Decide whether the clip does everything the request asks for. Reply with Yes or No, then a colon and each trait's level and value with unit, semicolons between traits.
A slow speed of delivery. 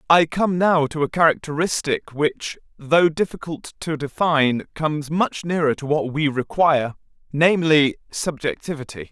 Yes: slow, 130 wpm